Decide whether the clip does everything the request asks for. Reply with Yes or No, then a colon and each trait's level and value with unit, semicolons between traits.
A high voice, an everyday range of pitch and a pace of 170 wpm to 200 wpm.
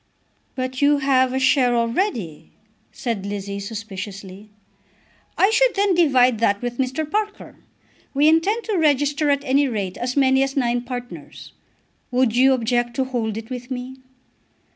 No: very high, 255 Hz; average, 3.6 semitones; average, 150 wpm